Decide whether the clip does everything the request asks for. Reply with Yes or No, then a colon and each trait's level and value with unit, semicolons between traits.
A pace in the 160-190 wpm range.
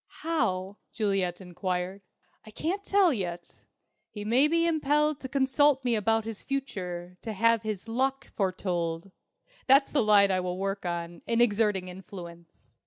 No: average, 150 wpm